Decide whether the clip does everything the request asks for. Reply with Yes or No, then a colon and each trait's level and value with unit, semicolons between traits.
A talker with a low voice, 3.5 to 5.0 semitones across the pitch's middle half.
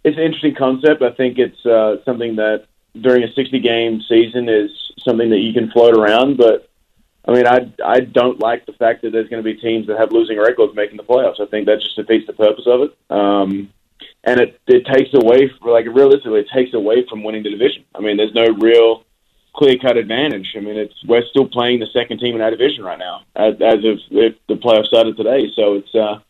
No: low, 115 Hz; narrow, 2.4 semitones